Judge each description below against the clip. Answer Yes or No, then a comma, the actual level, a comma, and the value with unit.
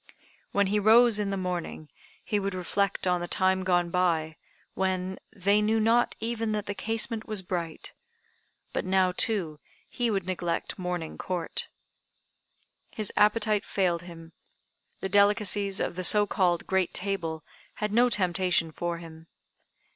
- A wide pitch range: No, average, 3.0 semitones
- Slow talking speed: No, average, 145 wpm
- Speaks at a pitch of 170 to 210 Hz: Yes, high, 190 Hz